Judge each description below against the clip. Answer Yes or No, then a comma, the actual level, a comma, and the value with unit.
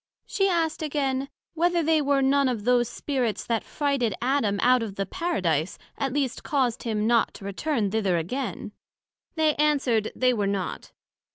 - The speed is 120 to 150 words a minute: No, average, 170 wpm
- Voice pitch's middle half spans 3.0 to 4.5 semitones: No, average, 5.1 semitones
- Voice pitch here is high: Yes, very high, 255 Hz